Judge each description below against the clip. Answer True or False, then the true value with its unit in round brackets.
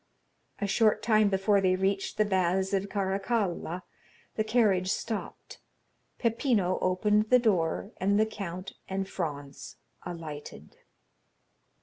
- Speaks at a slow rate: True (115 wpm)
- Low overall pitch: False (195 Hz)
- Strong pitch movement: False (2.5 semitones)